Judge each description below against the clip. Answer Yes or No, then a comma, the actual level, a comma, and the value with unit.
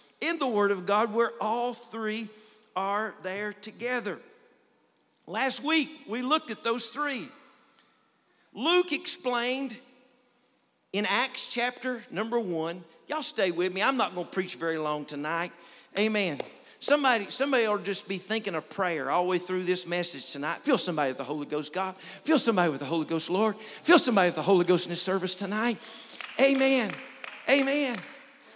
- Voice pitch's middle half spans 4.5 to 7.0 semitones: Yes, wide, 5.5 semitones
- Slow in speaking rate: No, average, 170 wpm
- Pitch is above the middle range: Yes, high, 215 Hz